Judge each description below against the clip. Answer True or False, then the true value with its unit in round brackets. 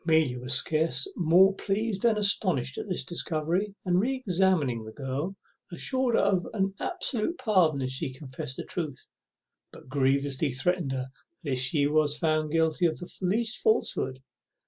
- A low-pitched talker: False (160 Hz)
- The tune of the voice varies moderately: False (6.1 semitones)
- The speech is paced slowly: False (160 wpm)